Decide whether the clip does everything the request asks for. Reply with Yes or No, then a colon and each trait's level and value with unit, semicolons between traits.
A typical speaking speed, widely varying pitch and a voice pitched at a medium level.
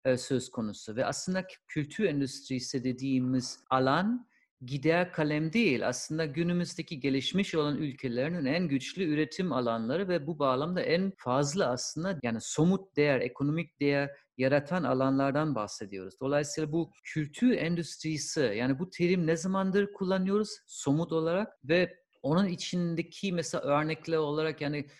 No: average, 125 wpm; average, 4.4 semitones; medium, 155 Hz